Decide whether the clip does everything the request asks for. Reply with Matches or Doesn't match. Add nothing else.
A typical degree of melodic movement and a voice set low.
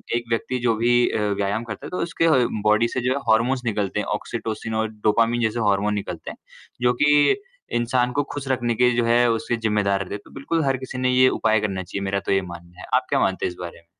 Matches